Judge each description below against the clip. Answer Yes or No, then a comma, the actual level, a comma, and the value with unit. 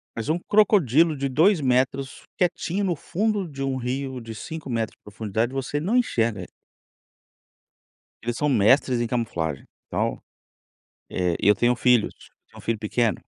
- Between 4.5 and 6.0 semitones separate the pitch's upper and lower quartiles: Yes, wide, 5.5 semitones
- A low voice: Yes, low, 130 Hz